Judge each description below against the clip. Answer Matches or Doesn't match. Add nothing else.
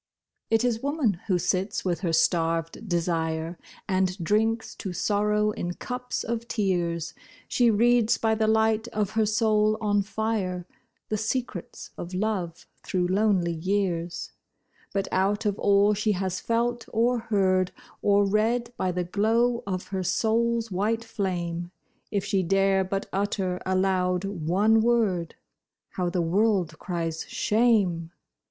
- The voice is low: Doesn't match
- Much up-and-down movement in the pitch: Doesn't match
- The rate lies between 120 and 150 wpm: Matches